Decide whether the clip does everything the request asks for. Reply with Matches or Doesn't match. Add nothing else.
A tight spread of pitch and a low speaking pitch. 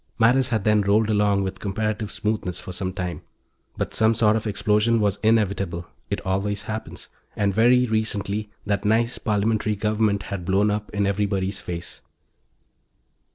Matches